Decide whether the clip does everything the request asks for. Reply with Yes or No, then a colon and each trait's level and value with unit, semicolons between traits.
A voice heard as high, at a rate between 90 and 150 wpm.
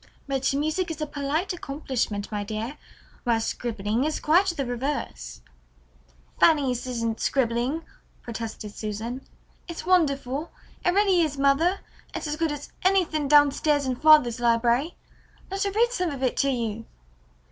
Yes: very high, 275 Hz; average, 145 wpm